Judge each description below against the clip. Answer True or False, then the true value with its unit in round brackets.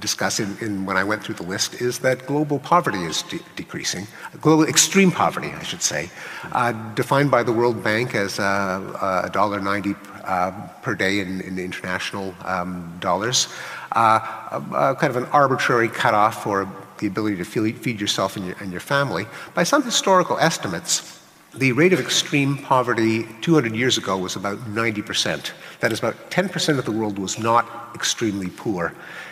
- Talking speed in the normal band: True (180 wpm)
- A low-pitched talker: True (110 Hz)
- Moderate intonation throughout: False (5.9 semitones)